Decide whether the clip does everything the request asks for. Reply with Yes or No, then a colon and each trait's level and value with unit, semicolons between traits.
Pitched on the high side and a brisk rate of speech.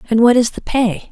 Yes: high, 230 Hz; fast, 270 wpm